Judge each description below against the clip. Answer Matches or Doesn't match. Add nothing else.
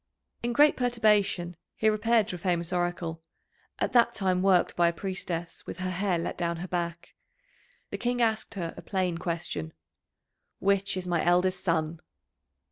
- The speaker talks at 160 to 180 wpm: Matches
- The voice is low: Doesn't match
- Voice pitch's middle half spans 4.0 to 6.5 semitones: Doesn't match